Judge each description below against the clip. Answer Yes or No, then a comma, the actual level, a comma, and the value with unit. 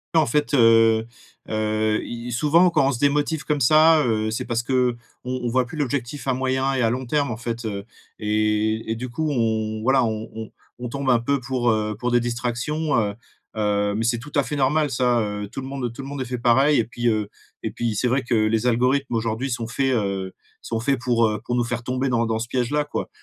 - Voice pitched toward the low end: Yes, low, 120 Hz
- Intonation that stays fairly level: No, average, 3.2 semitones